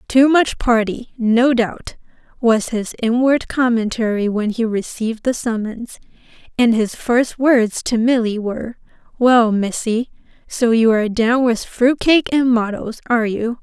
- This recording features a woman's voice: Yes, female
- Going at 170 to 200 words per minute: No, average, 150 wpm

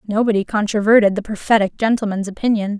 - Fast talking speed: No, slow, 130 wpm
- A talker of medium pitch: No, high, 210 Hz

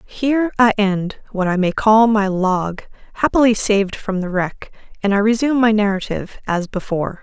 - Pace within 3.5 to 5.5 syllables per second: Yes, 5.2 syllables/s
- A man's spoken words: No, female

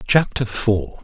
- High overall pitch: No, low, 120 Hz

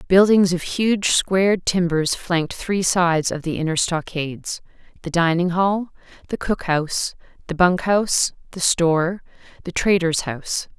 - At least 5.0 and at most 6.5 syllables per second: No, 4.6 syllables/s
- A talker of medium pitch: Yes, medium, 175 Hz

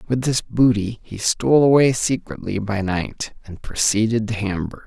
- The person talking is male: Yes, male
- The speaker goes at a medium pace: Yes, average, 160 wpm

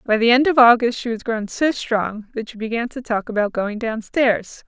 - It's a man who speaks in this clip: No, female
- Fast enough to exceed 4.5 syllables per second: Yes, 4.9 syllables/s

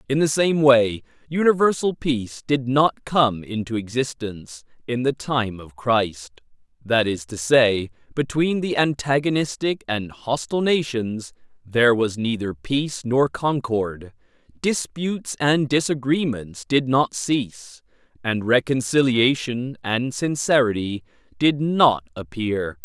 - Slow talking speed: Yes, slow, 115 wpm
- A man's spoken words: Yes, male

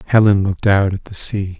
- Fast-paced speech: Yes, fast, 225 wpm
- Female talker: No, male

